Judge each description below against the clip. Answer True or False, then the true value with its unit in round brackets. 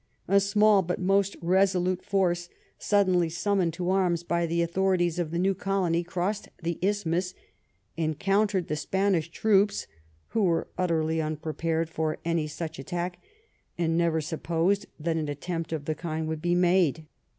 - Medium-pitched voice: True (175 Hz)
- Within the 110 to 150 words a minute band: False (160 wpm)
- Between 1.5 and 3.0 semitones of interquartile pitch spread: True (2.7 semitones)